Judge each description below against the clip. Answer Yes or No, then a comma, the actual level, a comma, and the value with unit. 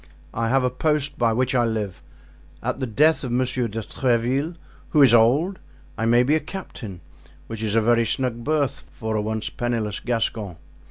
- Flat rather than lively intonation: No, average, 3.4 semitones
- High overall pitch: No, low, 120 Hz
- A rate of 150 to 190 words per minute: Yes, average, 185 wpm